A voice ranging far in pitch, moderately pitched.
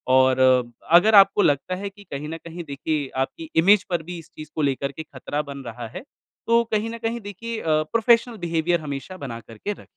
Yes: wide, 6.5 semitones; medium, 165 Hz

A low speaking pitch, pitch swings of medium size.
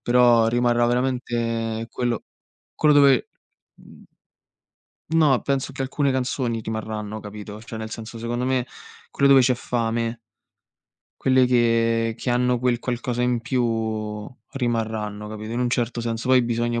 No: low, 120 Hz; narrow, 1.8 semitones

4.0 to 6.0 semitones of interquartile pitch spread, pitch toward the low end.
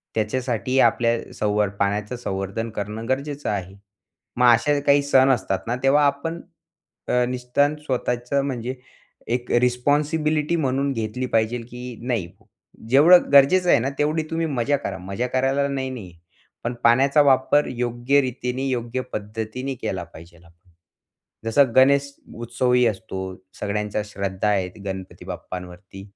Yes: average, 4.7 semitones; low, 125 Hz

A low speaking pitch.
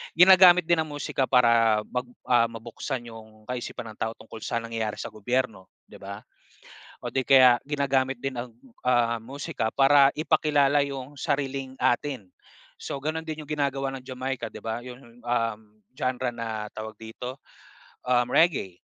Yes: low, 125 Hz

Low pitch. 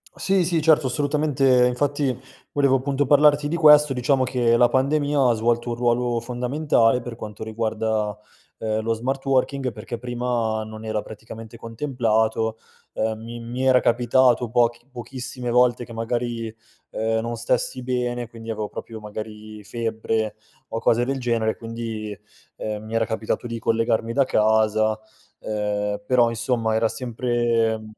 Yes: low, 120 Hz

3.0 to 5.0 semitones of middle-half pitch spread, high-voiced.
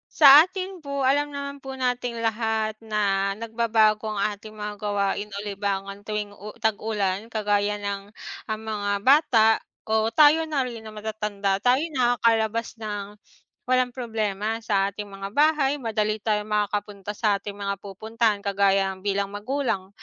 No: narrow, 2.4 semitones; high, 215 Hz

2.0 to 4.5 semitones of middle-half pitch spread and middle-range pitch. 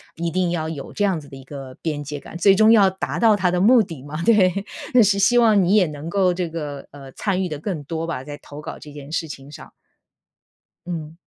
No: average, 4.9 semitones; medium, 170 Hz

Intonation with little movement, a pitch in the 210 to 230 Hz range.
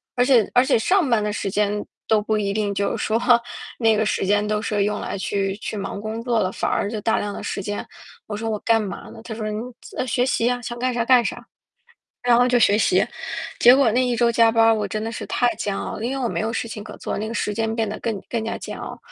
Yes: narrow, 2.3 semitones; high, 220 Hz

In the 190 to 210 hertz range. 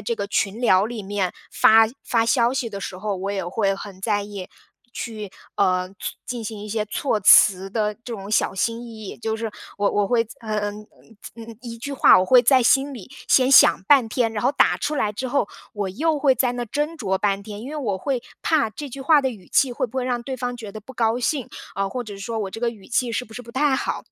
No: high, 225 Hz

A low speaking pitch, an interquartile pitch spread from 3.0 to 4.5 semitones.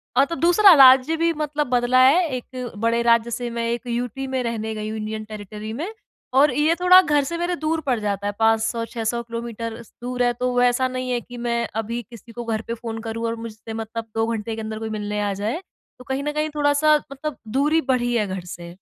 No: high, 240 Hz; average, 3.5 semitones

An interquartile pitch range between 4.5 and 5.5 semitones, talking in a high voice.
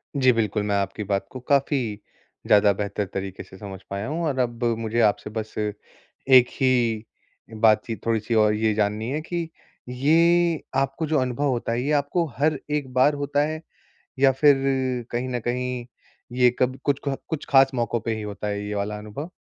No: average, 4.8 semitones; low, 120 Hz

